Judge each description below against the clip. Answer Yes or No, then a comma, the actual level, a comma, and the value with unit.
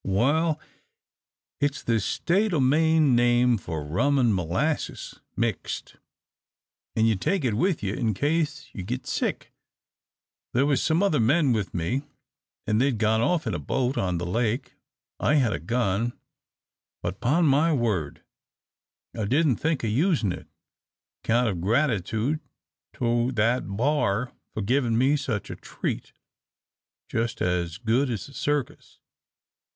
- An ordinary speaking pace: Yes, average, 145 wpm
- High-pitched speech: No, low, 120 Hz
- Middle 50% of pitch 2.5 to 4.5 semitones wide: No, average, 5.1 semitones